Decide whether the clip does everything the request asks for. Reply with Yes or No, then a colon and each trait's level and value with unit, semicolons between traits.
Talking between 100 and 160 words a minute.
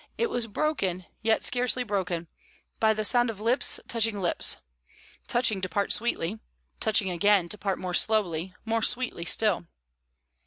Yes: average, 150 wpm